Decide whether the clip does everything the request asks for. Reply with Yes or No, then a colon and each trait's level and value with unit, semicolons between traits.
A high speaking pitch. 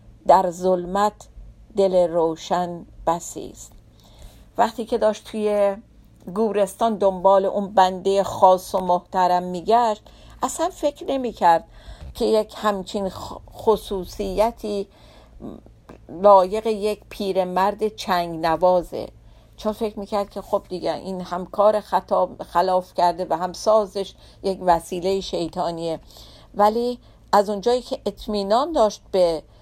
Yes: high, 195 Hz